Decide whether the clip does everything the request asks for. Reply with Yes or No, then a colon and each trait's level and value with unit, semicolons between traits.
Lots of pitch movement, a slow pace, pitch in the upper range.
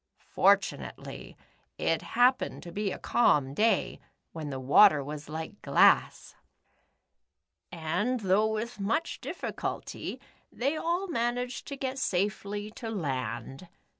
Yes: wide, 7.8 semitones; slow, 125 wpm; high, 205 Hz